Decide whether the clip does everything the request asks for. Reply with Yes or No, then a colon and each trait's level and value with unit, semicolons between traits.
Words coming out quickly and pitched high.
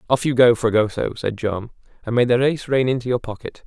No: fast, 230 wpm; low, 120 Hz